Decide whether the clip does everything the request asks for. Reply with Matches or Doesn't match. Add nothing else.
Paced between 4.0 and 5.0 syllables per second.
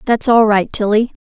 Matches